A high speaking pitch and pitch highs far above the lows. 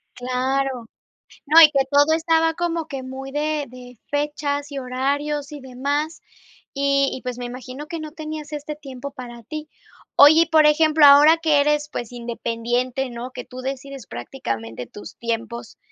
No: very high, 280 Hz; average, 3.1 semitones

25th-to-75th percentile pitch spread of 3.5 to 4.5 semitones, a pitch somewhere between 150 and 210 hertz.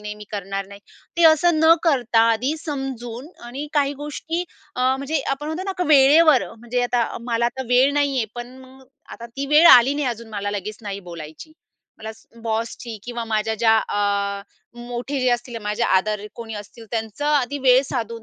No: average, 4.2 semitones; high, 240 Hz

